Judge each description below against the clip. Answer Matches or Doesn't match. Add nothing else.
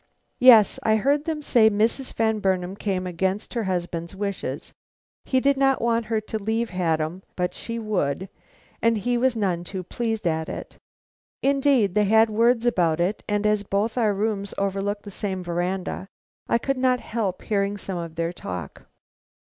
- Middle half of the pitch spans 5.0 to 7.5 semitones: Doesn't match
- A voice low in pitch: Doesn't match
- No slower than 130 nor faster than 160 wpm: Doesn't match